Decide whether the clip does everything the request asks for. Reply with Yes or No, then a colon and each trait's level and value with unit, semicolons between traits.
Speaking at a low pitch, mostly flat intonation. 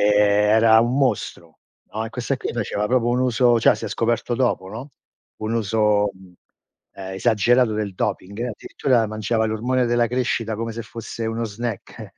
Yes: low, 115 Hz; narrow, 2.3 semitones